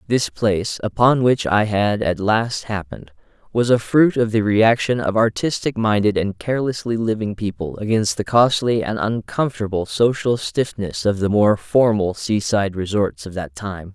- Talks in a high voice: No, low, 105 Hz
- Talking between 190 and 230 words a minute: No, average, 165 wpm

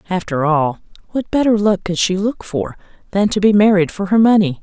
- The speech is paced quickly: Yes, fast, 210 wpm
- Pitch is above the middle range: Yes, high, 195 Hz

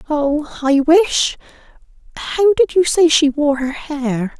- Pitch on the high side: Yes, very high, 300 Hz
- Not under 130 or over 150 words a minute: Yes, slow, 135 wpm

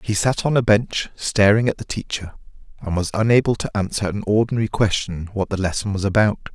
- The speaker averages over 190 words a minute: Yes, average, 200 wpm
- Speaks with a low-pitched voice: Yes, low, 105 Hz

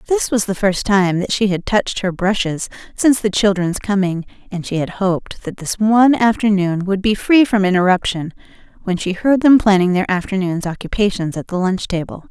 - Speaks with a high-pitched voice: Yes, high, 195 Hz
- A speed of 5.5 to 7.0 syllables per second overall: No, 5.3 syllables/s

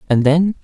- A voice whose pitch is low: No, medium, 155 Hz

